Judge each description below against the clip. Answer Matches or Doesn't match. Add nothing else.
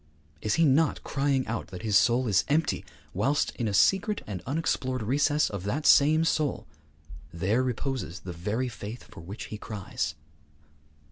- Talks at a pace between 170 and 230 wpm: Doesn't match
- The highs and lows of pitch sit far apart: Matches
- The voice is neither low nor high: Doesn't match